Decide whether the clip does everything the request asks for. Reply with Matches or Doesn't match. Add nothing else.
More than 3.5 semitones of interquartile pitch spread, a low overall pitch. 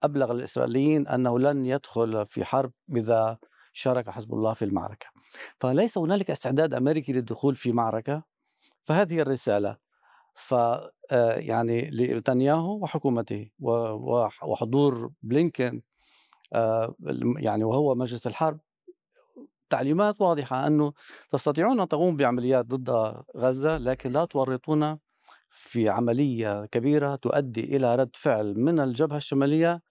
Matches